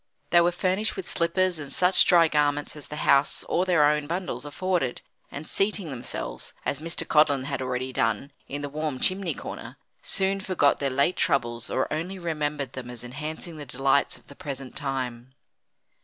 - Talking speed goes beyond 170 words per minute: Yes, average, 180 wpm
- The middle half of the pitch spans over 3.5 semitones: Yes, average, 4.2 semitones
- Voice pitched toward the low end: No, medium, 150 Hz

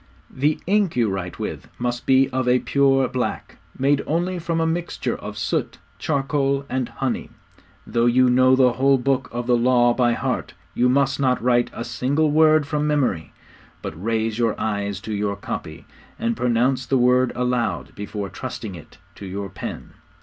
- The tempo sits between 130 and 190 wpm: Yes, average, 175 wpm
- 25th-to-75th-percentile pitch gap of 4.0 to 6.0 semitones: No, average, 2.9 semitones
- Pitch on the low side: Yes, low, 125 Hz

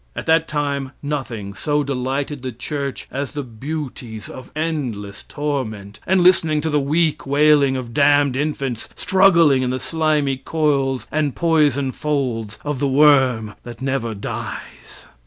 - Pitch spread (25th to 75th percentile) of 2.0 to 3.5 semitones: Yes, average, 2.9 semitones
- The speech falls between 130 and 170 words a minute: Yes, average, 145 wpm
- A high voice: No, medium, 140 Hz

